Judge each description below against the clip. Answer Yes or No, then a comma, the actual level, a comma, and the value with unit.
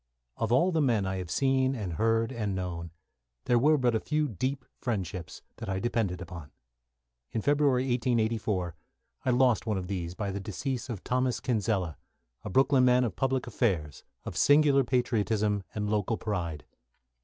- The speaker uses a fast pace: No, average, 165 wpm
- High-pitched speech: No, low, 115 Hz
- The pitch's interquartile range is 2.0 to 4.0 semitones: No, average, 5.2 semitones